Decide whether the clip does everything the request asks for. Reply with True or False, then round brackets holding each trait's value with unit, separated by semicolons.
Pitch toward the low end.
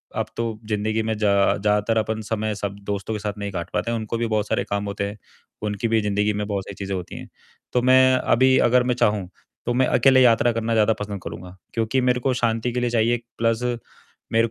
True (110 Hz)